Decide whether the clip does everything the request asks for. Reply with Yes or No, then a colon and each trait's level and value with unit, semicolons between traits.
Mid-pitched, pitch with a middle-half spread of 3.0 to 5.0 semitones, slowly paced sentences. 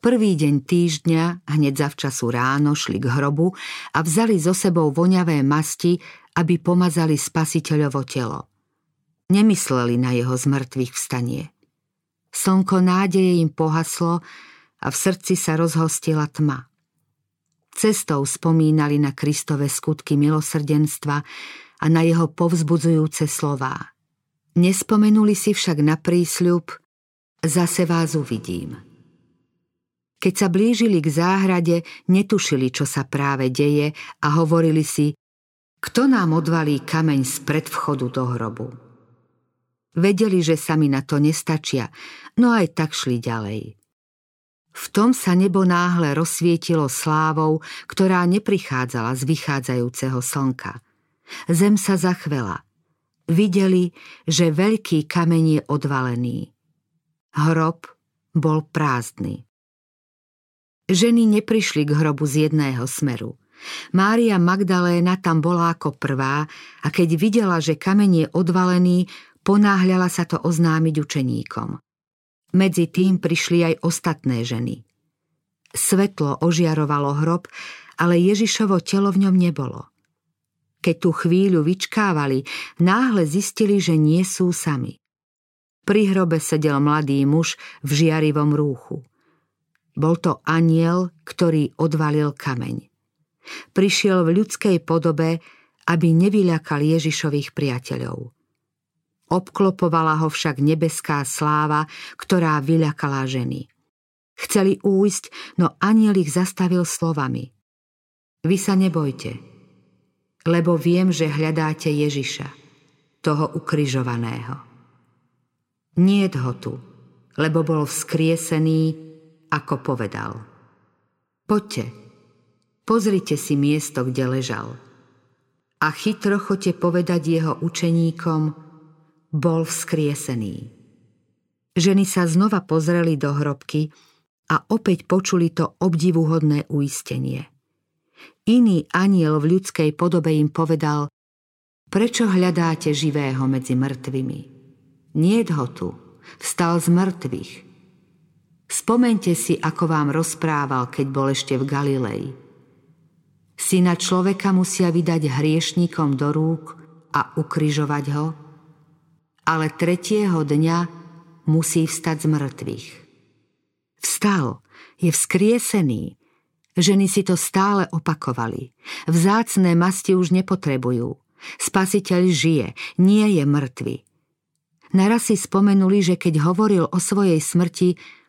Yes: medium, 160 Hz; average, 3.6 semitones; slow, 105 wpm